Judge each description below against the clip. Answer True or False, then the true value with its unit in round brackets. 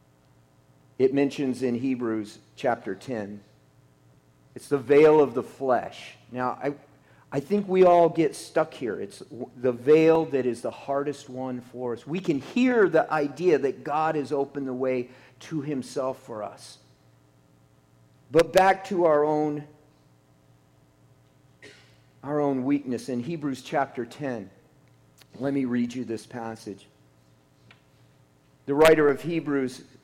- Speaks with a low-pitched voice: True (130 Hz)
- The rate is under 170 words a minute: True (135 wpm)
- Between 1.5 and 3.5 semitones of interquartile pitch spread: False (5.6 semitones)